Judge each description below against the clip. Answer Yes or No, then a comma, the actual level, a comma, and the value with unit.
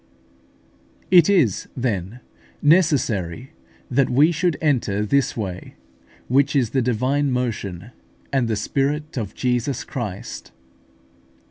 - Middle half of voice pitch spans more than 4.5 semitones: Yes, average, 5.0 semitones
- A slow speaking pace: Yes, slow, 110 wpm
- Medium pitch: No, low, 125 Hz